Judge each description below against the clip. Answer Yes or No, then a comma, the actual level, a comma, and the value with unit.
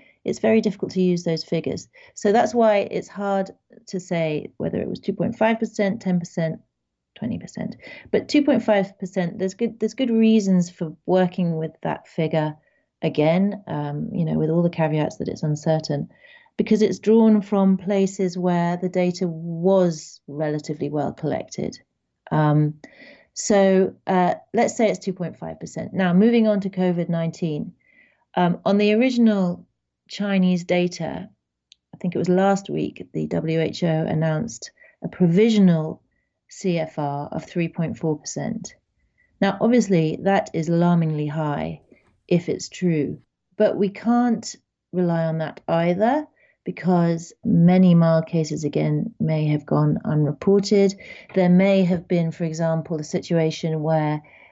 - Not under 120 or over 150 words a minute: Yes, average, 145 wpm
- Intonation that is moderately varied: Yes, average, 3.9 semitones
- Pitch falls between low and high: Yes, medium, 180 Hz